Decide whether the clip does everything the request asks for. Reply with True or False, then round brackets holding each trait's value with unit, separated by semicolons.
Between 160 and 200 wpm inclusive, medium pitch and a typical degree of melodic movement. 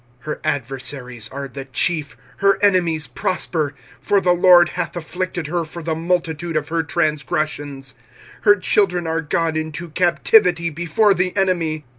False (150 wpm; 165 Hz; 3.0 semitones)